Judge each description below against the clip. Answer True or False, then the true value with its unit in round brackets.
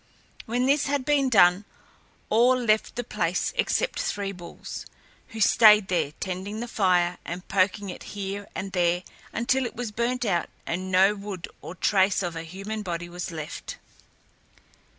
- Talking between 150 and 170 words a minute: True (160 wpm)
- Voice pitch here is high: True (195 Hz)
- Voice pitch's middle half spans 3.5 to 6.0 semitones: True (4.0 semitones)